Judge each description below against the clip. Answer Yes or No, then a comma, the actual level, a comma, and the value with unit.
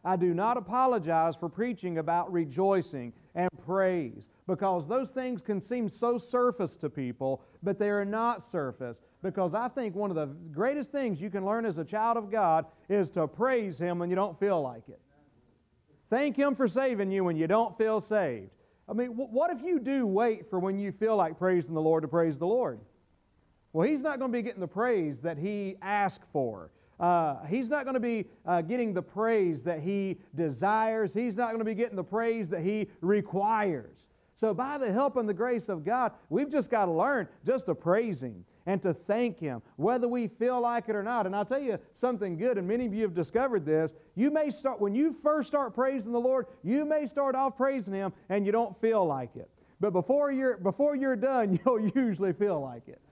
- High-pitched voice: Yes, high, 205 Hz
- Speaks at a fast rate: Yes, fast, 215 wpm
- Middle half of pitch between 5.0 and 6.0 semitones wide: Yes, wide, 5.4 semitones